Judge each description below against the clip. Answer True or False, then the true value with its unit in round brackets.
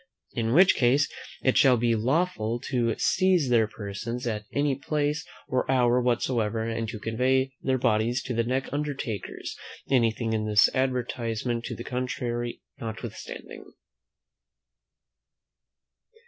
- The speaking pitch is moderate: False (120 Hz)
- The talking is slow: True (125 wpm)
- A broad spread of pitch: False (2.6 semitones)